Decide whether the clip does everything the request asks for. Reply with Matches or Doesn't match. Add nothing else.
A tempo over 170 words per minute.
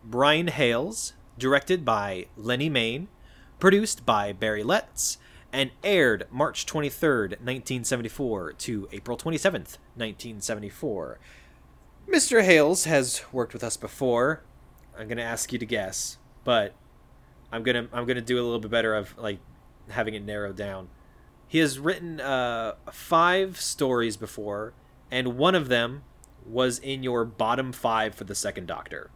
Doesn't match